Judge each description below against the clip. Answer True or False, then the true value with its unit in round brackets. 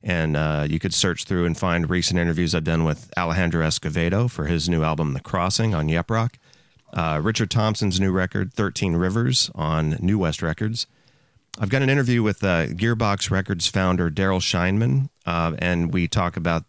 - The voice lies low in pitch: True (90 Hz)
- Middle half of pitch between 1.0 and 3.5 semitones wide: False (4.6 semitones)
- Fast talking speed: False (185 wpm)